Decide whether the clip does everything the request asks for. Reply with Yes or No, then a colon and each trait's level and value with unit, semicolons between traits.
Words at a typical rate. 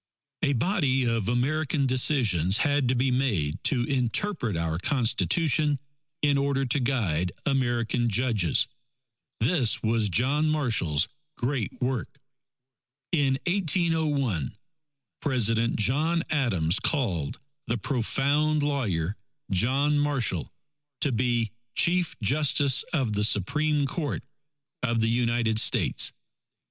No: slow, 110 wpm